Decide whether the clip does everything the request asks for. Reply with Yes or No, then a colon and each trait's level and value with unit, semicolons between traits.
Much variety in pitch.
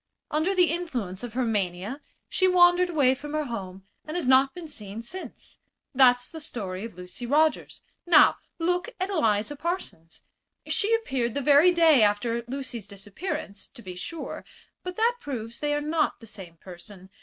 Yes: wide, 8.0 semitones